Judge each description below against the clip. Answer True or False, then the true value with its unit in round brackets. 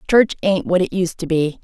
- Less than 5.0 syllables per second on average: False (5.1 syllables/s)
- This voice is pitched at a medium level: True (180 Hz)